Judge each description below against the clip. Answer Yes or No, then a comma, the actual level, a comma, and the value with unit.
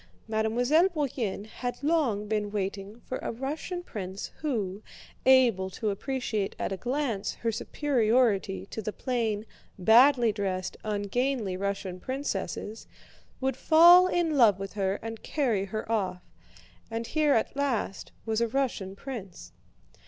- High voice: Yes, high, 225 Hz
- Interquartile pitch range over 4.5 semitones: Yes, average, 5.0 semitones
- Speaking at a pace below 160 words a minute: Yes, slow, 135 wpm